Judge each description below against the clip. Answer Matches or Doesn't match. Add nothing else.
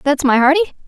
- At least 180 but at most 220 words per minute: Matches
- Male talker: Doesn't match